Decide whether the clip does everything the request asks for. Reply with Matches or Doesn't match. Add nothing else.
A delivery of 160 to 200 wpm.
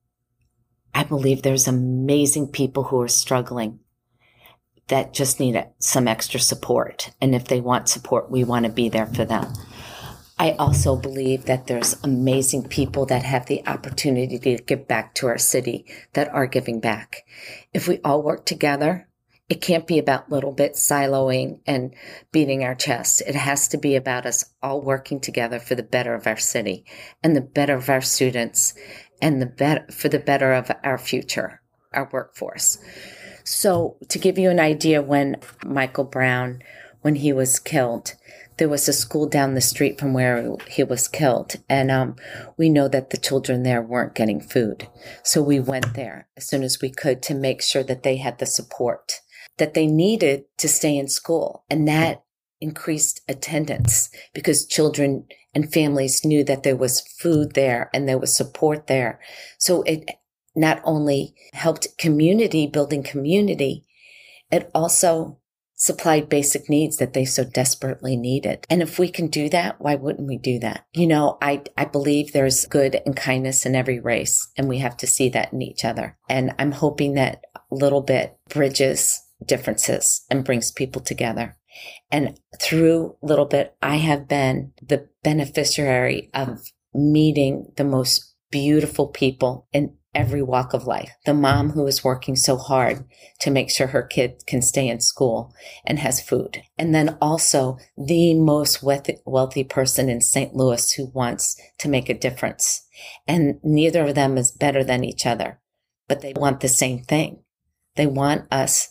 Matches